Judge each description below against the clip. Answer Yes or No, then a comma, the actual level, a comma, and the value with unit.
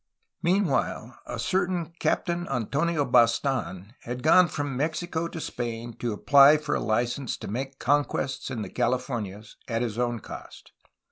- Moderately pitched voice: No, low, 130 Hz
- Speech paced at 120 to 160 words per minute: Yes, average, 145 wpm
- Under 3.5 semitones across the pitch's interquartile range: No, average, 4.7 semitones